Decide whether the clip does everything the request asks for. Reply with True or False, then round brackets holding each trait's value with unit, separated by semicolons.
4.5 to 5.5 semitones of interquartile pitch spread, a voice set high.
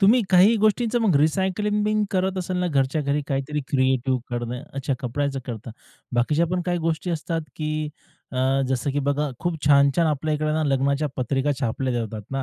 False (4.8 semitones; 150 Hz)